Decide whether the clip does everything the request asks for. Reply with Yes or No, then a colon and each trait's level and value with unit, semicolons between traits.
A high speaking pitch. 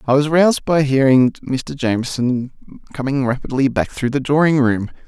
No: low, 135 Hz